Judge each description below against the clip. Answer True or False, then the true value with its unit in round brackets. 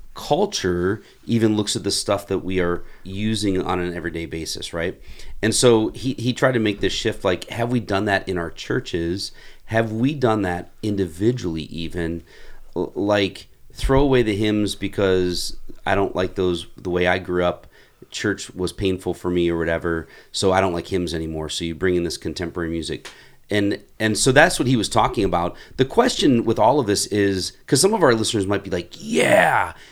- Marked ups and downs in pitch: False (3.5 semitones)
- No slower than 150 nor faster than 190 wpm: False (200 wpm)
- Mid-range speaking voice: False (95 Hz)